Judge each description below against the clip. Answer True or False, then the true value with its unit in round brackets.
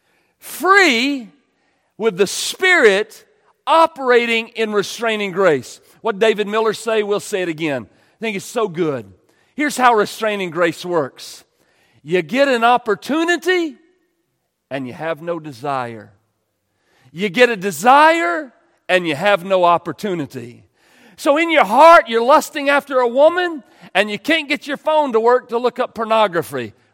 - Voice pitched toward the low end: False (225 Hz)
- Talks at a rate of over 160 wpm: False (145 wpm)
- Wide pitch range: True (8.5 semitones)